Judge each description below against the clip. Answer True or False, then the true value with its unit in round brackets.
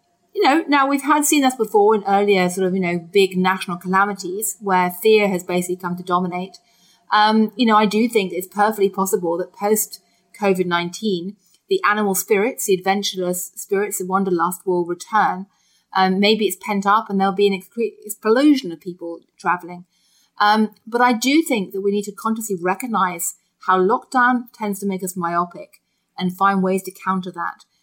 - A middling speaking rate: True (180 wpm)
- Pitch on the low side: False (195 Hz)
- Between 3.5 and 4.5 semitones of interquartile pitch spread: False (2.7 semitones)